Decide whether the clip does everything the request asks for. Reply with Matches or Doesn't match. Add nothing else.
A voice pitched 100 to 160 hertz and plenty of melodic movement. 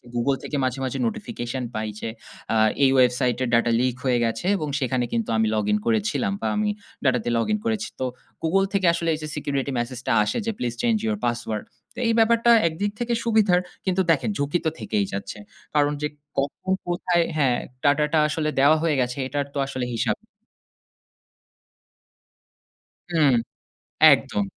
Matches